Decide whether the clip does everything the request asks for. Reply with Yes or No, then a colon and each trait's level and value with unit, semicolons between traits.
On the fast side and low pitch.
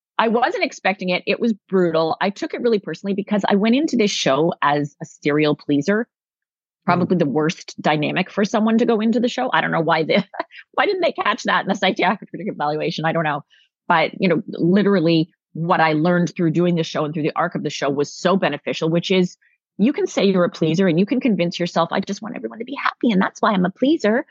No: fast, 240 wpm; medium, 185 Hz